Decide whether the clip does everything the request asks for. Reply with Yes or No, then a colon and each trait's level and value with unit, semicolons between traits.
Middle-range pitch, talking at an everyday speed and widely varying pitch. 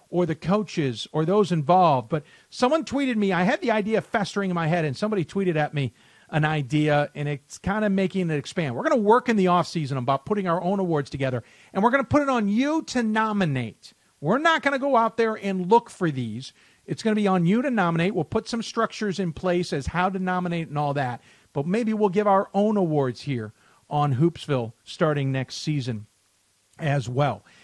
No: medium, 175 Hz; fast, 220 wpm; wide, 6.5 semitones